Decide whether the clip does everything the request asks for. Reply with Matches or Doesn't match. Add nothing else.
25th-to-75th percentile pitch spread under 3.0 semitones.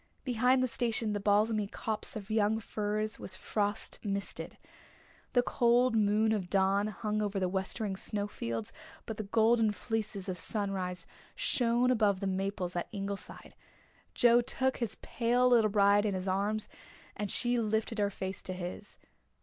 Matches